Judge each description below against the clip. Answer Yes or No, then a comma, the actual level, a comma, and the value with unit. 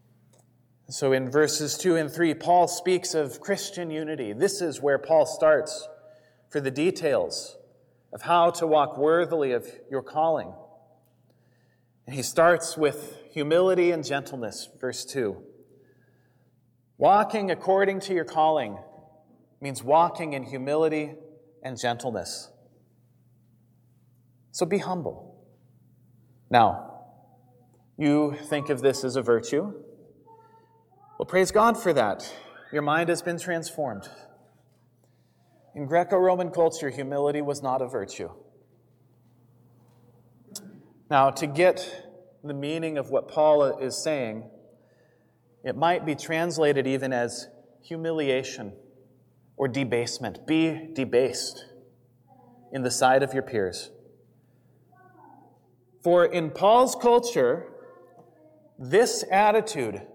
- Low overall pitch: No, medium, 145 Hz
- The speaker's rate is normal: No, slow, 110 wpm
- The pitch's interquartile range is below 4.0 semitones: No, average, 5.2 semitones